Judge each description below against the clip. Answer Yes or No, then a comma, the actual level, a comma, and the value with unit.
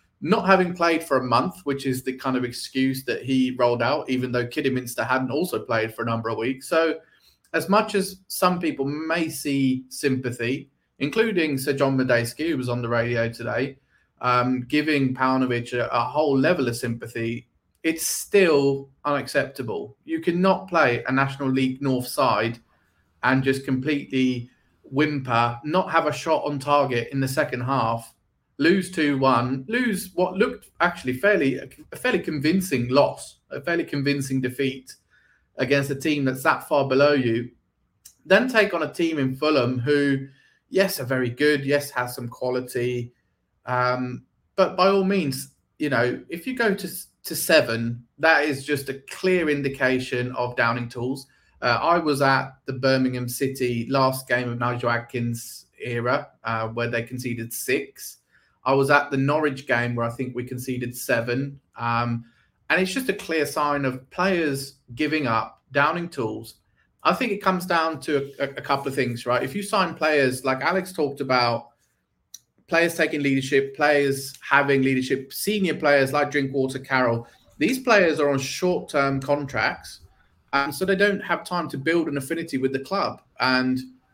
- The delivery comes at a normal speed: Yes, average, 170 wpm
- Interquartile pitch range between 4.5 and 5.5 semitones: No, average, 3.7 semitones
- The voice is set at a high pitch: No, low, 135 Hz